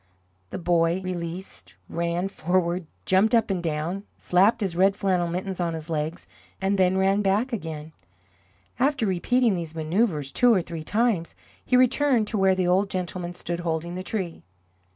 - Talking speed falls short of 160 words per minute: No, average, 165 wpm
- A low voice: No, medium, 185 Hz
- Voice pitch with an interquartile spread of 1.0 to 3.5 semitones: Yes, average, 2.8 semitones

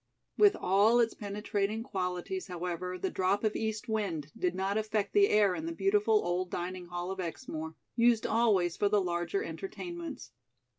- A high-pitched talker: Yes, high, 205 Hz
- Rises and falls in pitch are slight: No, average, 4.5 semitones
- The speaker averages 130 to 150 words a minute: No, average, 165 wpm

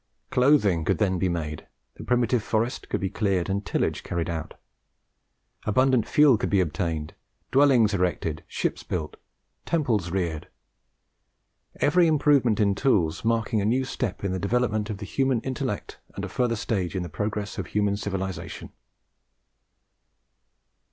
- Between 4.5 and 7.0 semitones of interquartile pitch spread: Yes, average, 5.2 semitones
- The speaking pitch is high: No, low, 105 Hz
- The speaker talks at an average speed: Yes, average, 145 wpm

